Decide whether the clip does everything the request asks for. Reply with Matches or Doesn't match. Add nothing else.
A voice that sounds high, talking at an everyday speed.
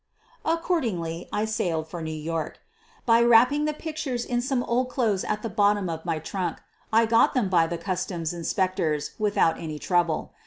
Matches